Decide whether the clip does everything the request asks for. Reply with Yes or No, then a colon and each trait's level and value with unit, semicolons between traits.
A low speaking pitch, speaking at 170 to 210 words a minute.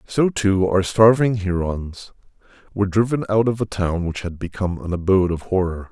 Yes: very low, 95 Hz; average, 185 wpm